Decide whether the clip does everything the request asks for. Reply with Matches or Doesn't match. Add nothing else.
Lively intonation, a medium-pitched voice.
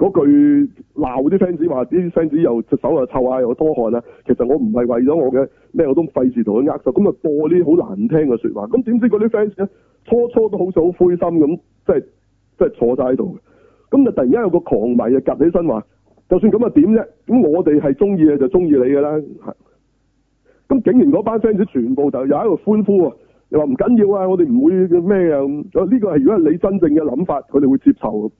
Matches